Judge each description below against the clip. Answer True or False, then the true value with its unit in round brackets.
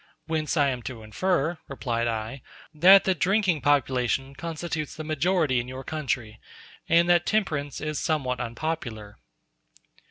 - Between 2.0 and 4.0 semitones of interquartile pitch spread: False (4.6 semitones)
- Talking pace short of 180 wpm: True (135 wpm)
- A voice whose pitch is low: False (145 Hz)